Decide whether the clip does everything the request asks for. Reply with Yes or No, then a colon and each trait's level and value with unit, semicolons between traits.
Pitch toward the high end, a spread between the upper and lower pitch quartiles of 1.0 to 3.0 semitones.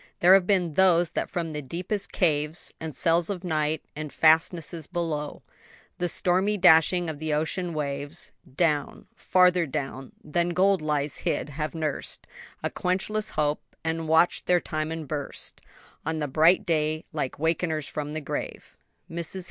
No: medium, 160 Hz; average, 2.7 semitones